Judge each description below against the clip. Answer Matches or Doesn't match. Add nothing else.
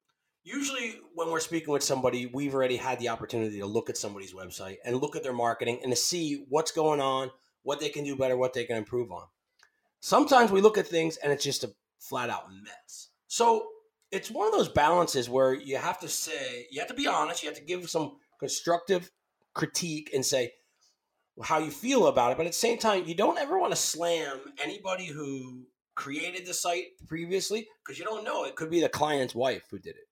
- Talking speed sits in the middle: Doesn't match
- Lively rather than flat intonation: Matches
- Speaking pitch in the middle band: Matches